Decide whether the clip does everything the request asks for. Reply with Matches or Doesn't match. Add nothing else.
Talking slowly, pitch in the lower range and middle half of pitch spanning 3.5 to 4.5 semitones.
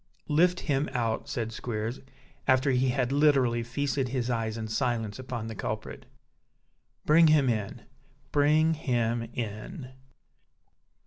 Matches